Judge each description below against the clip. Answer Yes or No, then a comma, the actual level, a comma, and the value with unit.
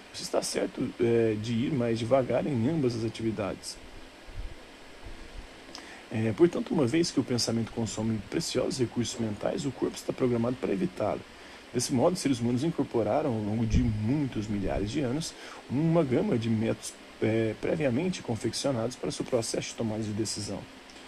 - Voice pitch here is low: Yes, low, 115 Hz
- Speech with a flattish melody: Yes, narrow, 2.3 semitones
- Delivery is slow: No, average, 155 wpm